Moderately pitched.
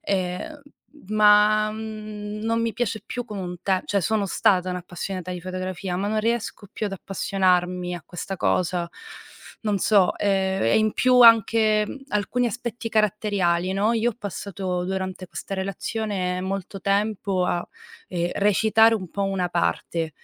No: high, 195 Hz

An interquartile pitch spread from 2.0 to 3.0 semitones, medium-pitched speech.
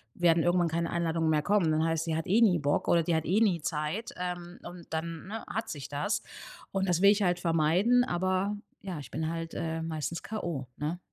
Yes: average, 2.7 semitones; medium, 170 Hz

